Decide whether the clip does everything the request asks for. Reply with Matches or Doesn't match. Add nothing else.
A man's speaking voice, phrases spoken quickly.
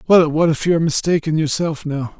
Matches